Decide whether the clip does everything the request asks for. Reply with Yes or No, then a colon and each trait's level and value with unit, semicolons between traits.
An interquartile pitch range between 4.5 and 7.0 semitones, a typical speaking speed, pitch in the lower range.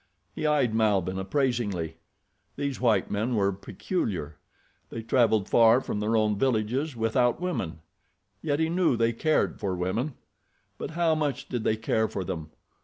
Yes: average, 5.1 semitones; average, 155 wpm; low, 115 Hz